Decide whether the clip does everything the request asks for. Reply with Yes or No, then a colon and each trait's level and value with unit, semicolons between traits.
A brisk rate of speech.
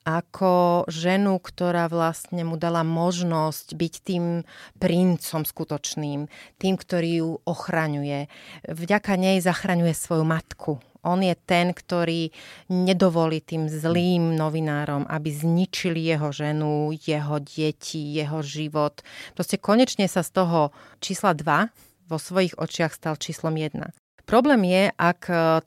No: average, 120 wpm